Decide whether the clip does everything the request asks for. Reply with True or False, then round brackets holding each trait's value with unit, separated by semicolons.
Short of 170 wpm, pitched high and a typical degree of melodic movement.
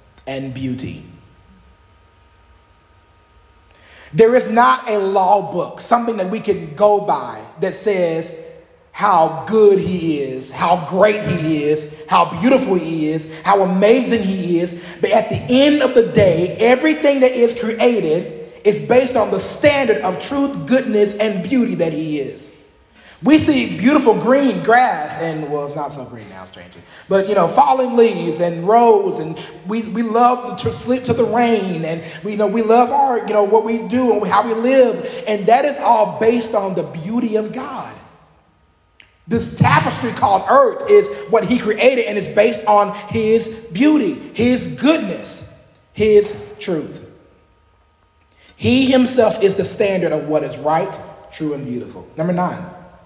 False (160 wpm; 205 Hz; 6.9 semitones)